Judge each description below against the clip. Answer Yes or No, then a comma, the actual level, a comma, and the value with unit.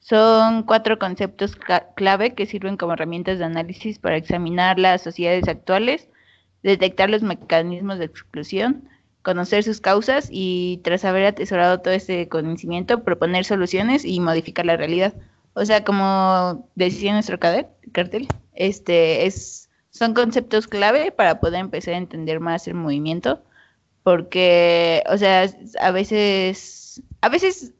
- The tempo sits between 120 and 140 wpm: Yes, average, 135 wpm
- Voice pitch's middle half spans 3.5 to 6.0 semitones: No, average, 3.1 semitones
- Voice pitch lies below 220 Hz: Yes, medium, 185 Hz